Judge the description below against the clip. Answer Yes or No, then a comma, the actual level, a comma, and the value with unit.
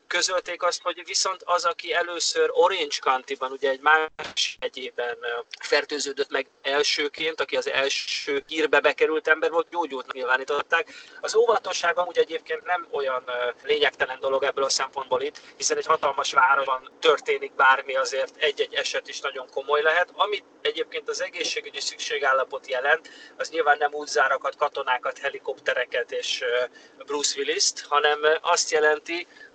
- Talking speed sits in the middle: Yes, average, 140 wpm